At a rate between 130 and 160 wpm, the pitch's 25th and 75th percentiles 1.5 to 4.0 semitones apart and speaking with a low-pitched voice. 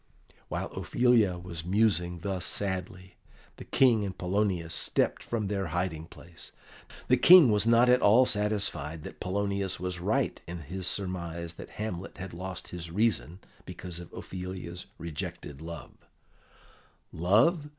Yes: average, 140 wpm; average, 3.2 semitones; very low, 95 Hz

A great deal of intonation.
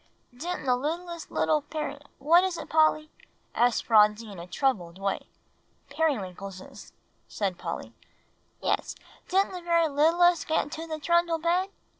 Yes: wide, 7.1 semitones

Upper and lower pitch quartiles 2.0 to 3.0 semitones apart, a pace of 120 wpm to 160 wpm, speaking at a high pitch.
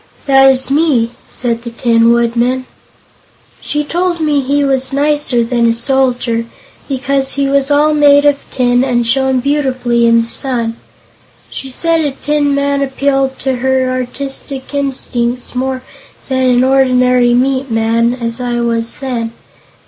Yes: narrow, 2.6 semitones; average, 150 wpm; very high, 260 Hz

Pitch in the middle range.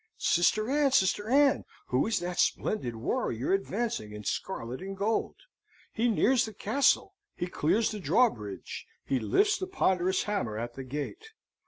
No: high, 195 Hz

